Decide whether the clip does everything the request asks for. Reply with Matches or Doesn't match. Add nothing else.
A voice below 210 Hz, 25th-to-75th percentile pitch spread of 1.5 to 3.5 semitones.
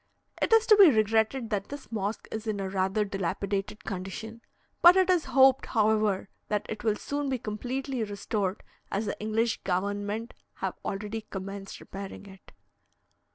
Doesn't match